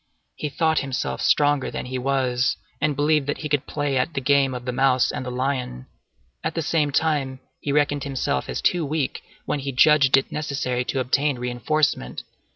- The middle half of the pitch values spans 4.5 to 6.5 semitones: No, narrow, 2.4 semitones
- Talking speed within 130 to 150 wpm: No, average, 190 wpm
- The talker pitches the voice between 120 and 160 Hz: Yes, medium, 140 Hz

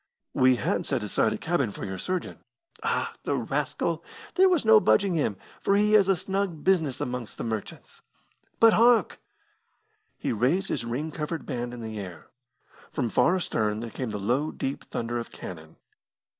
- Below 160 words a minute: No, average, 175 wpm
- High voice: No, low, 135 Hz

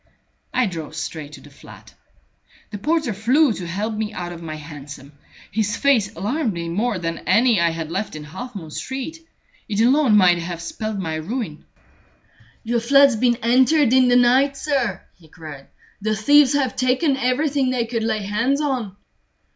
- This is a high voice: Yes, high, 220 Hz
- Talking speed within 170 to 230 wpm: Yes, average, 175 wpm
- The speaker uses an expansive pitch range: Yes, wide, 7.0 semitones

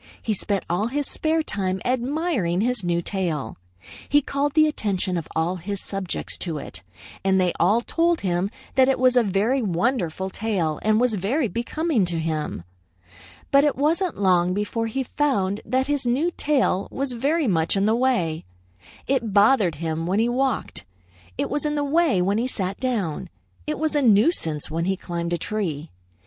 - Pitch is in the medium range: No, high, 215 Hz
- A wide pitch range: Yes, wide, 6.9 semitones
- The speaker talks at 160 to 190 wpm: Yes, average, 180 wpm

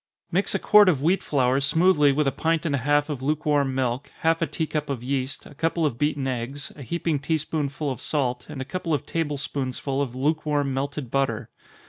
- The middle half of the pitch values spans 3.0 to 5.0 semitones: No, narrow, 2.6 semitones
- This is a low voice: No, medium, 145 Hz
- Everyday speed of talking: No, fast, 220 wpm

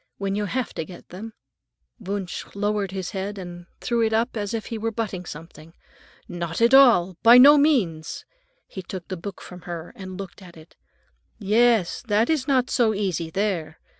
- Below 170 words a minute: No, average, 185 wpm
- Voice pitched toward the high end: Yes, high, 200 Hz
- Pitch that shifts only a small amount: No, average, 4.3 semitones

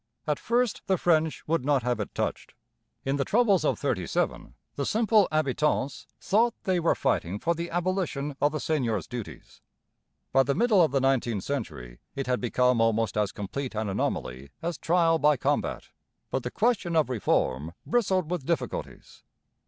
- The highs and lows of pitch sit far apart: Yes, wide, 6.2 semitones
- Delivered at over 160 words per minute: Yes, average, 170 wpm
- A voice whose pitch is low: No, medium, 145 Hz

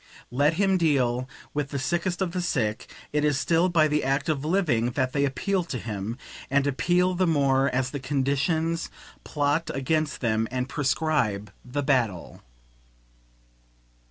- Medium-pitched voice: Yes, medium, 145 Hz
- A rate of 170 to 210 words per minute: No, average, 155 wpm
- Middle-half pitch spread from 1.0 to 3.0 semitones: No, average, 4.1 semitones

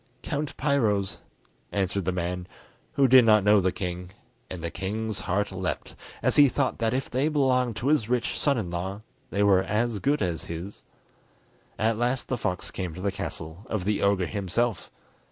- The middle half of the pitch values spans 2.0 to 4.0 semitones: No, average, 4.8 semitones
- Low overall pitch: Yes, low, 105 Hz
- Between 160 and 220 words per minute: Yes, average, 185 wpm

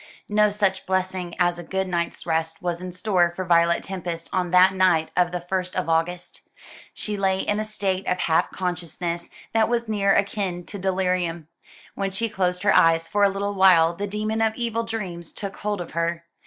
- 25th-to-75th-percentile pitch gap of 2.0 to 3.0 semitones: Yes, narrow, 2.6 semitones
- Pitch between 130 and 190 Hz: Yes, medium, 185 Hz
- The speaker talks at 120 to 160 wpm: No, average, 195 wpm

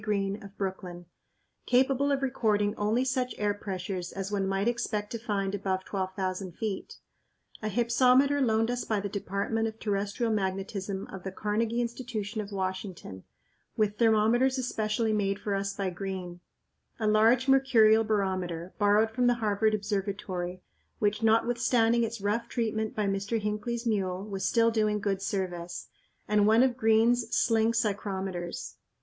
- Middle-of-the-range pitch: No, high, 210 Hz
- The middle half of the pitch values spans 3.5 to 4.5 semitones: No, average, 2.8 semitones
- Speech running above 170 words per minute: No, average, 150 wpm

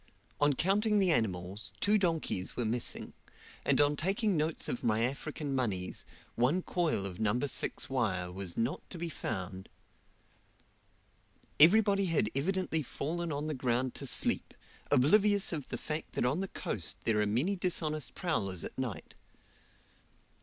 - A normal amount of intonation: No, wide, 7.6 semitones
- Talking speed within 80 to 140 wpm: No, average, 150 wpm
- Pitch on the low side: No, medium, 145 Hz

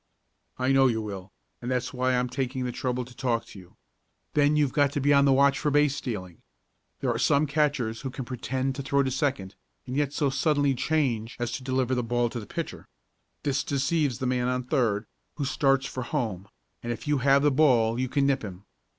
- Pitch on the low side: Yes, low, 130 Hz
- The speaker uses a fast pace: Yes, fast, 220 wpm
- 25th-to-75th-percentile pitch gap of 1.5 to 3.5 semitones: Yes, narrow, 2.6 semitones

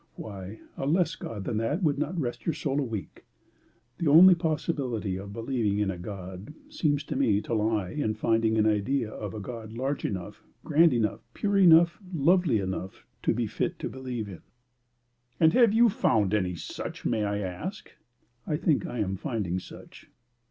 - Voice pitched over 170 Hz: No, low, 115 Hz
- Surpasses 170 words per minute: Yes, average, 180 wpm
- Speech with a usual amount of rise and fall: No, wide, 6.6 semitones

